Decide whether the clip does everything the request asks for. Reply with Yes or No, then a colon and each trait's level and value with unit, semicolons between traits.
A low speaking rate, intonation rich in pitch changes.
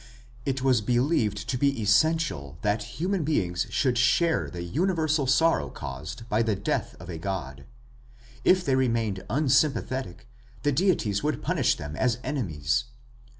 No: average, 145 wpm; wide, 7.2 semitones